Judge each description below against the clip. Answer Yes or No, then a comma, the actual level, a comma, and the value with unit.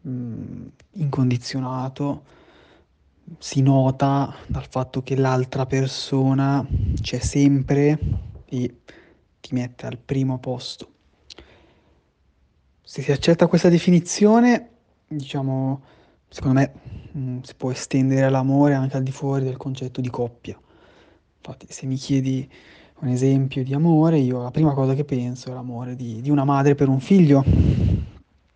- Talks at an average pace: Yes, average, 130 wpm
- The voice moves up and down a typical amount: No, narrow, 2.1 semitones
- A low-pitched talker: Yes, low, 130 Hz